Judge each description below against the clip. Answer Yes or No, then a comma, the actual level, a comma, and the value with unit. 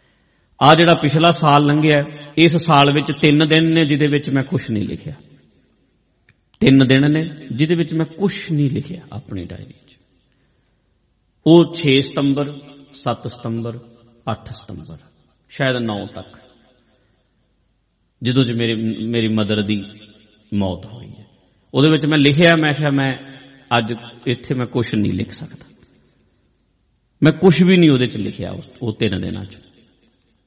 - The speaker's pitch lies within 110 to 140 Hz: Yes, low, 135 Hz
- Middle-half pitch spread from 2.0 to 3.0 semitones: No, average, 5.1 semitones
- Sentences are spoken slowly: No, average, 145 wpm